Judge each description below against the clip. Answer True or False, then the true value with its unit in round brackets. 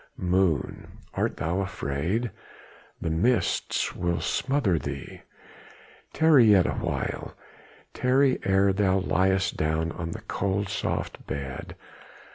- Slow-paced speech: True (105 wpm)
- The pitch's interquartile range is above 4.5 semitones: False (3.9 semitones)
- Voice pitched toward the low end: True (95 Hz)